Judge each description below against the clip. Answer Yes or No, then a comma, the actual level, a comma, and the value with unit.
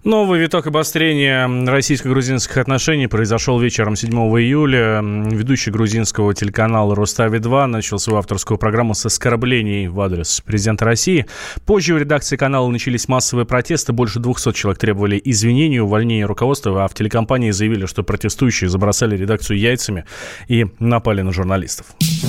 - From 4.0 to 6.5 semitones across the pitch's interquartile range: No, average, 3.6 semitones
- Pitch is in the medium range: No, low, 115 Hz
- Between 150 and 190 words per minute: No, average, 135 wpm